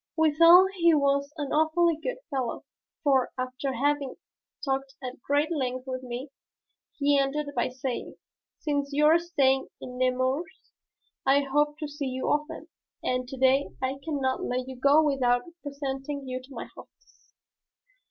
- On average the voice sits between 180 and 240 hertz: No, very high, 275 Hz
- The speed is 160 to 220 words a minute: No, average, 150 wpm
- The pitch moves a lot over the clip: No, narrow, 2.4 semitones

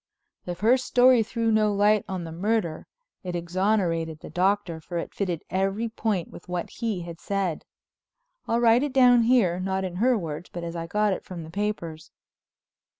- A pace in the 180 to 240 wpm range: Yes, average, 190 wpm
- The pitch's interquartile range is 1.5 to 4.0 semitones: No, average, 4.4 semitones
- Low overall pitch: No, high, 190 Hz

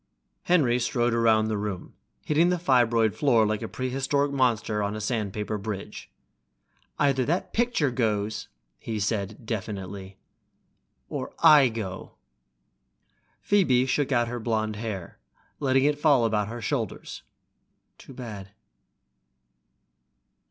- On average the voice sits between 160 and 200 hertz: No, low, 115 Hz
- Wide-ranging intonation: No, average, 4.0 semitones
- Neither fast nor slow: No, slow, 125 wpm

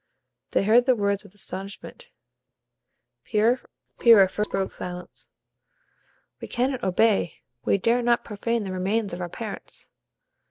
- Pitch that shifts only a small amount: No, average, 3.5 semitones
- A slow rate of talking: Yes, slow, 125 wpm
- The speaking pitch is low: No, high, 210 Hz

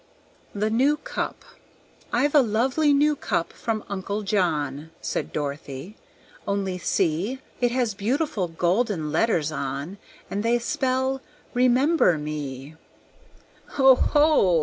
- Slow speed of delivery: Yes, slow, 110 wpm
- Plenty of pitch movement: Yes, wide, 8.2 semitones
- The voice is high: Yes, high, 210 Hz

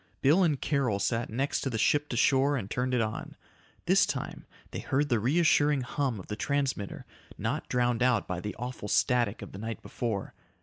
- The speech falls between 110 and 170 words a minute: No, average, 200 wpm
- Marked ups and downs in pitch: No, average, 4.2 semitones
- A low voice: Yes, low, 125 Hz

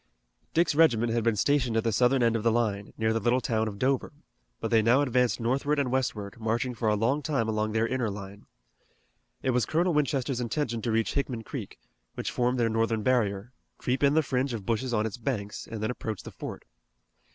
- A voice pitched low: Yes, low, 115 Hz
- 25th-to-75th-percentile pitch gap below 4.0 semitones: Yes, average, 2.8 semitones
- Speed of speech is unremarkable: No, fast, 215 wpm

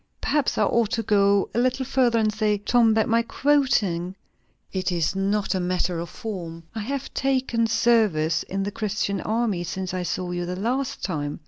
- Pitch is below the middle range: No, high, 210 Hz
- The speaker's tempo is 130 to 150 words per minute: No, average, 190 wpm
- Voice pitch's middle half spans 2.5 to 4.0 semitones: No, average, 4.4 semitones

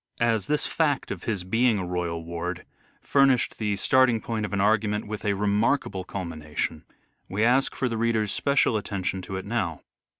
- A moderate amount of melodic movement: Yes, average, 3.9 semitones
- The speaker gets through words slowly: No, average, 175 wpm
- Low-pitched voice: Yes, low, 105 Hz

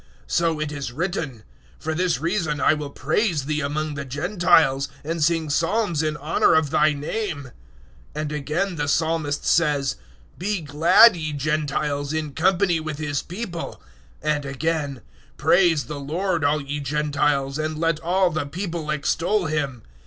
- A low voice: No, medium, 155 Hz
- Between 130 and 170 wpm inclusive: Yes, average, 160 wpm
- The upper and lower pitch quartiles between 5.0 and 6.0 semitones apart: No, narrow, 2.6 semitones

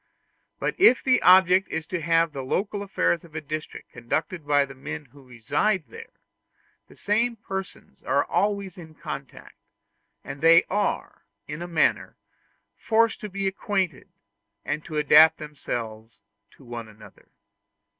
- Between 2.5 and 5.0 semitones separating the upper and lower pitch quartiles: No, wide, 5.4 semitones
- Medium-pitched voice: Yes, medium, 160 Hz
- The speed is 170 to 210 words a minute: No, average, 145 wpm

